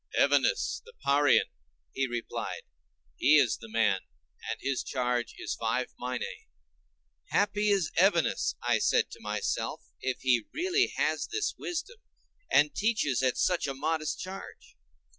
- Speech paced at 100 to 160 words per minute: Yes, average, 140 wpm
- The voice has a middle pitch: Yes, medium, 145 Hz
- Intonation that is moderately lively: No, wide, 8.3 semitones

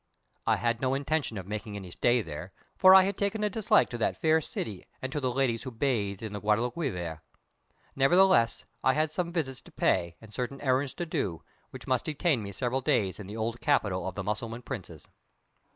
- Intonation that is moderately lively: No, wide, 5.8 semitones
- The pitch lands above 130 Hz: No, low, 120 Hz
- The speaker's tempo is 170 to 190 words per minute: No, fast, 205 wpm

